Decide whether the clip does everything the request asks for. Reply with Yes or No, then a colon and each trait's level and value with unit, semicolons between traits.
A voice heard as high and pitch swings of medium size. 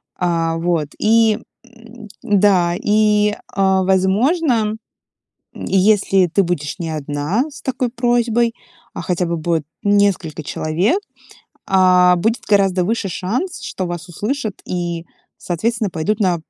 Yes: high, 195 Hz; average, 4.2 semitones